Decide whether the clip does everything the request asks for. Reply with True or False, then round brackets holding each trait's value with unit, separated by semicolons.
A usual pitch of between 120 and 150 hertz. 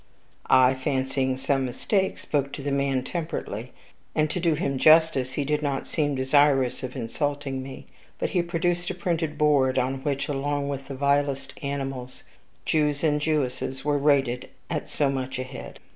True (140 Hz)